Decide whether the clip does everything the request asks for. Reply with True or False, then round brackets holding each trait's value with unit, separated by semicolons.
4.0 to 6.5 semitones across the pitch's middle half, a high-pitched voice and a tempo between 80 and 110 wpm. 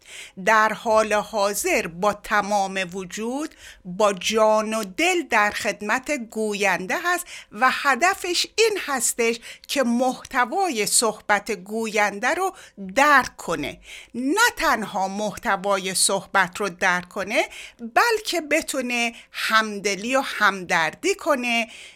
True (5.4 semitones; 220 Hz; 105 wpm)